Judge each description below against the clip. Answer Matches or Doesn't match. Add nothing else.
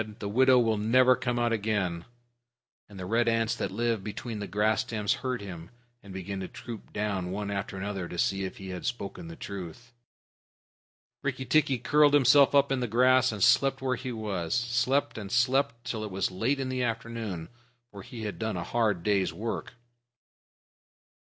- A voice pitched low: Matches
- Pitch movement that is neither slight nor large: Matches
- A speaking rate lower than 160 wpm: Doesn't match